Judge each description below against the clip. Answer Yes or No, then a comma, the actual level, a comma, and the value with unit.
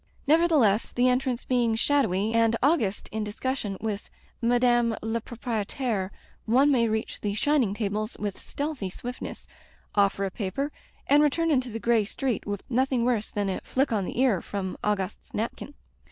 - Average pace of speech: Yes, average, 160 wpm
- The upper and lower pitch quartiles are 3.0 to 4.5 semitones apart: Yes, average, 4.0 semitones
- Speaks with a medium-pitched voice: No, high, 230 Hz